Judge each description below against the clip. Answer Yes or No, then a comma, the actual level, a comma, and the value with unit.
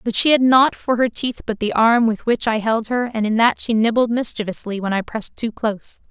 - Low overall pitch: No, high, 225 Hz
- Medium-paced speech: No, fast, 255 wpm